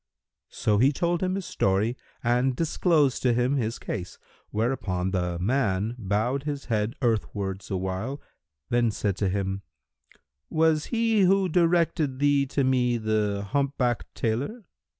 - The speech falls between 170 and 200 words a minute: No, slow, 135 wpm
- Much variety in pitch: Yes, wide, 5.8 semitones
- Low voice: Yes, low, 120 Hz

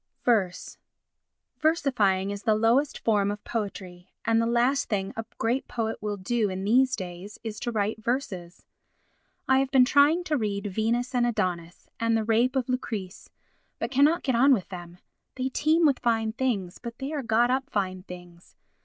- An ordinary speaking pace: Yes, average, 180 wpm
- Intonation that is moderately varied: Yes, average, 4.5 semitones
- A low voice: No, high, 225 Hz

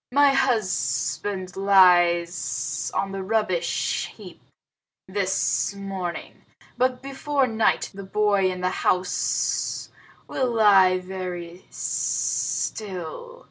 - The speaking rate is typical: No, slow, 95 wpm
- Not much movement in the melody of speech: No, average, 3.4 semitones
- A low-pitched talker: No, high, 195 Hz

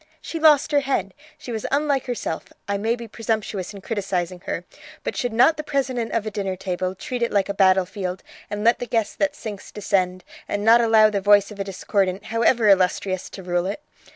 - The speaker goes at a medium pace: No, fast, 210 wpm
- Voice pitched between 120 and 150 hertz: No, high, 210 Hz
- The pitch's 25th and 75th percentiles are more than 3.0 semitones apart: Yes, average, 3.7 semitones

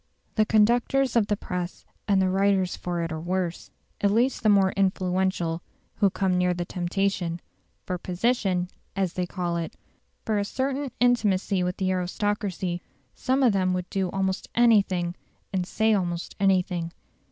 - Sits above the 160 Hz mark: Yes, high, 190 Hz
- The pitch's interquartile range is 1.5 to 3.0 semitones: Yes, narrow, 2.5 semitones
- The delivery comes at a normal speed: Yes, average, 160 wpm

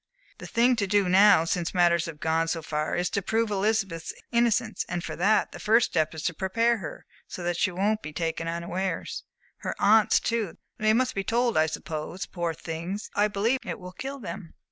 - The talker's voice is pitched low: No, high, 190 Hz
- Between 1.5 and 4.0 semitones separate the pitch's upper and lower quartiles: No, average, 4.6 semitones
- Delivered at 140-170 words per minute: No, fast, 205 wpm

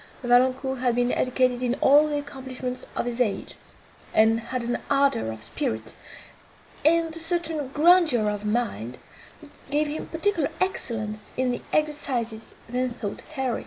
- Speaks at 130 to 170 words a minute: Yes, average, 150 wpm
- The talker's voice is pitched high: Yes, very high, 255 Hz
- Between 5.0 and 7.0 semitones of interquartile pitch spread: No, average, 4.0 semitones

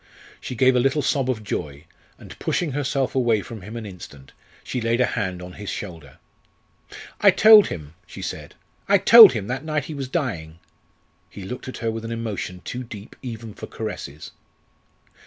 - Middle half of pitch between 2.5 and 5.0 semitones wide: No, wide, 5.5 semitones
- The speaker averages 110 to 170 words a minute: No, average, 185 wpm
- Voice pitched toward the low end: Yes, low, 115 Hz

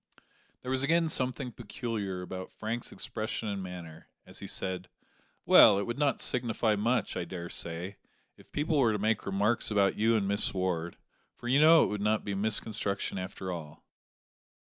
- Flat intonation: No, average, 4.2 semitones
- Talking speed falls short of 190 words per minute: Yes, average, 170 wpm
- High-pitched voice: No, low, 105 Hz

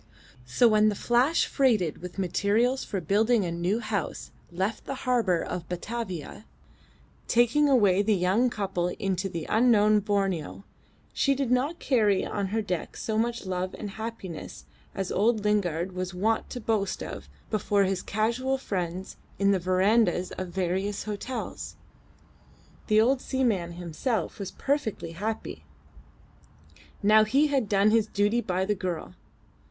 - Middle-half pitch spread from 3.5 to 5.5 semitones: Yes, average, 3.8 semitones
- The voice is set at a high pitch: Yes, high, 205 Hz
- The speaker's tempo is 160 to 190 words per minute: No, average, 145 wpm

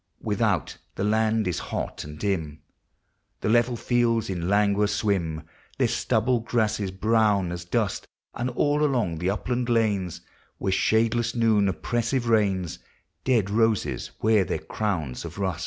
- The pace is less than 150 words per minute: Yes, average, 140 wpm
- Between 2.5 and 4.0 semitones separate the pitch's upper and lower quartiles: Yes, average, 3.7 semitones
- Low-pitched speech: Yes, low, 105 Hz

